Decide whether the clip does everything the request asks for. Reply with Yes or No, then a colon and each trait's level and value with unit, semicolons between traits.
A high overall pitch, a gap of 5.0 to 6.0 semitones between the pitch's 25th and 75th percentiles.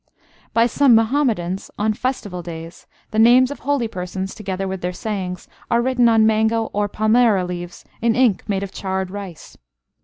No: high, 210 Hz; average, 3.8 semitones